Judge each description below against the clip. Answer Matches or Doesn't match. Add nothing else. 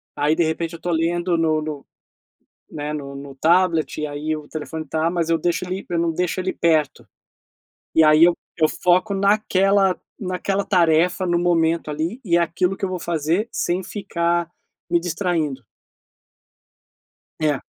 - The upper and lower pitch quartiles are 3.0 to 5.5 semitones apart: Doesn't match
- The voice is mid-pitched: Matches